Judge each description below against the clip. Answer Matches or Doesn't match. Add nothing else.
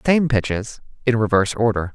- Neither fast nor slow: Matches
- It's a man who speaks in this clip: Matches